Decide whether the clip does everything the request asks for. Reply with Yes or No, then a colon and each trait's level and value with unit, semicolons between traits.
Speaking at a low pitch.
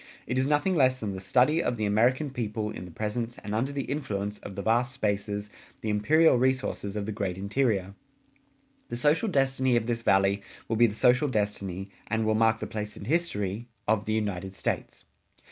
Yes: low, 110 Hz